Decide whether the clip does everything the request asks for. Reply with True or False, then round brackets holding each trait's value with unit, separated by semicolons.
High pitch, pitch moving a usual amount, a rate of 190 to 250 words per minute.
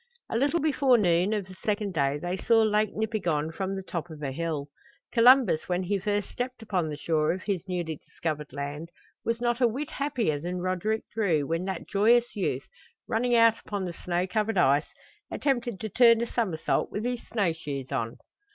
False (195 Hz; 5.7 semitones; 195 wpm)